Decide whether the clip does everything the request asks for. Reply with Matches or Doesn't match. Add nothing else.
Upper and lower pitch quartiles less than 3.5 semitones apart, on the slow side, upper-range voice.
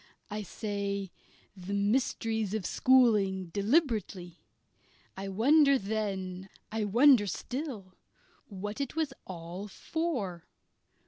Doesn't match